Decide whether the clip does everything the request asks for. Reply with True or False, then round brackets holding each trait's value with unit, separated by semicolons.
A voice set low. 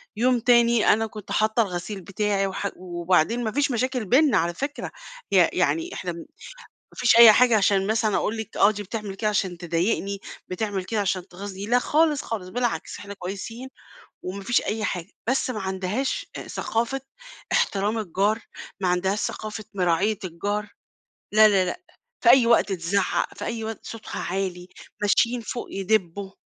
False (210 Hz)